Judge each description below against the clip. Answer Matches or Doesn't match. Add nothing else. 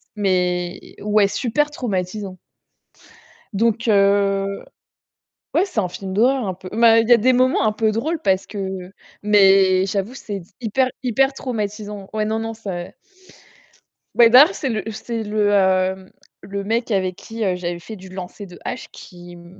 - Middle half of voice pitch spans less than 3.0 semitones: Doesn't match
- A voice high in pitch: Matches